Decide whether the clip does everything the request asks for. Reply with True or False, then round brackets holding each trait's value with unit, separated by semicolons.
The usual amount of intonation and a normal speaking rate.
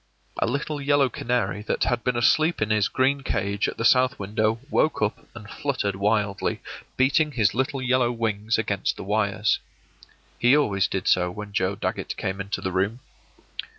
True (4.3 semitones; 175 wpm)